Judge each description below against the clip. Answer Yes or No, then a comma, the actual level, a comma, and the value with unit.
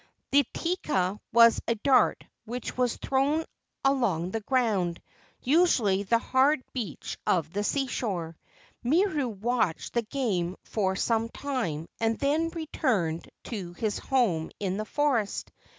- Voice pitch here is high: Yes, high, 230 Hz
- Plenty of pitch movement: Yes, wide, 6.0 semitones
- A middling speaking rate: No, slow, 130 wpm